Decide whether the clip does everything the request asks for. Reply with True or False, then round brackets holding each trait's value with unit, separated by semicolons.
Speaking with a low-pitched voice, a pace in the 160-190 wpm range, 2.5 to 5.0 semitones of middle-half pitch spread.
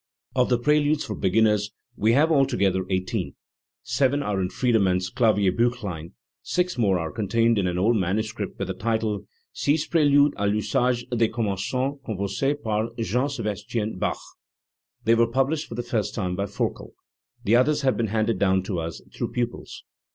True (110 Hz; 165 wpm; 4.2 semitones)